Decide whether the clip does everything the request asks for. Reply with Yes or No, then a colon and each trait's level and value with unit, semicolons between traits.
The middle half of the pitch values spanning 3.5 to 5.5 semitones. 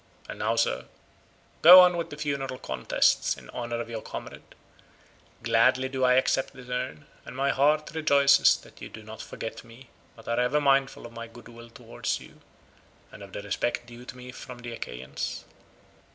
No: average, 2.8 semitones